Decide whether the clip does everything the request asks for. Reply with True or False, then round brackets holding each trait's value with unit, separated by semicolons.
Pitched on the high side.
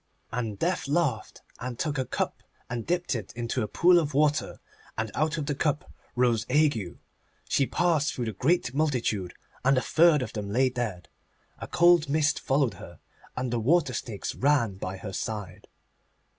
False (130 Hz)